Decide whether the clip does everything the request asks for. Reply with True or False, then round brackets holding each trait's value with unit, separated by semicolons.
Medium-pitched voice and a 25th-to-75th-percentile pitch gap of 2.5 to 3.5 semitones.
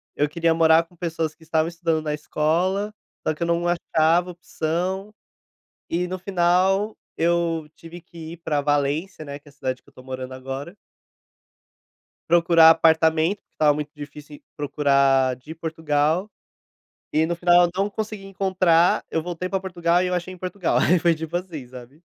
True (165 Hz; 2.8 semitones)